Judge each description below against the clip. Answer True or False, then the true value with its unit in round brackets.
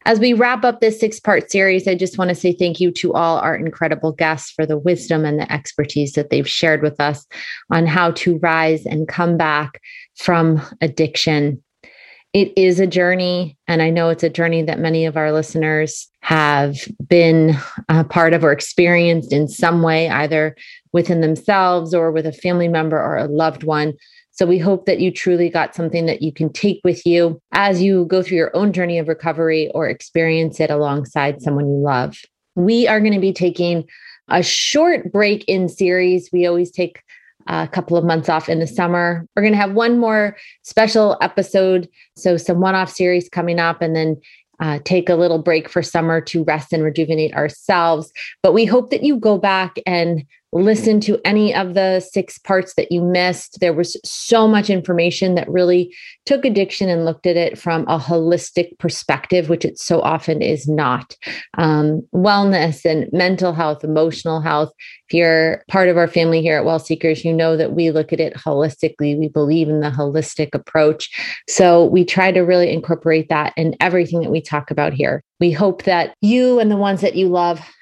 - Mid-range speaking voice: True (170 Hz)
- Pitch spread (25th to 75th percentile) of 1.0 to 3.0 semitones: True (2.5 semitones)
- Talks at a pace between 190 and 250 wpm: True (195 wpm)